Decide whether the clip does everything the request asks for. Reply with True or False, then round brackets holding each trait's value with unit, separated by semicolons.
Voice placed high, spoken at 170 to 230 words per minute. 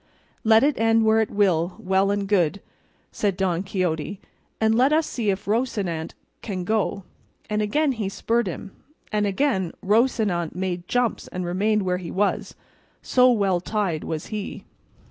False (200 Hz; 160 wpm)